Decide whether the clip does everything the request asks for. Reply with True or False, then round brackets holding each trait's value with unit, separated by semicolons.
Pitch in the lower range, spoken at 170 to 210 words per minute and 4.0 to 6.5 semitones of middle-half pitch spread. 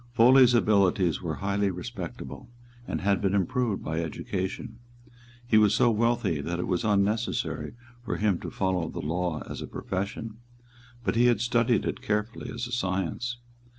False (105 Hz; 160 wpm; 4.3 semitones)